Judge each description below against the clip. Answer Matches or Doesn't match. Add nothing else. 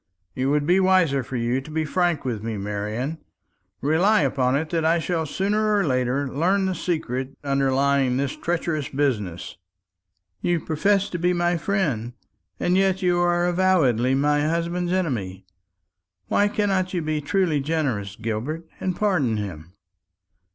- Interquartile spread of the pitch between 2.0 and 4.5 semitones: Doesn't match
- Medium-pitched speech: Matches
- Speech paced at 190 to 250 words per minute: Doesn't match